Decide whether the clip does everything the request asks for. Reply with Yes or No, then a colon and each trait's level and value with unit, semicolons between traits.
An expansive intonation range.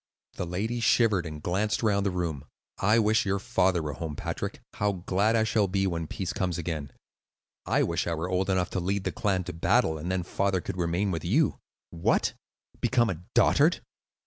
No: average, 2.9 semitones